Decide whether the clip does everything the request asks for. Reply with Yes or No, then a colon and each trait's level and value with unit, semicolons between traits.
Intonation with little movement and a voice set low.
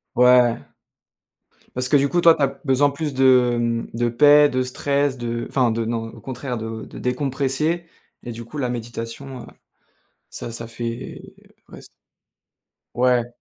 No: average, 3.0 semitones; low, 125 Hz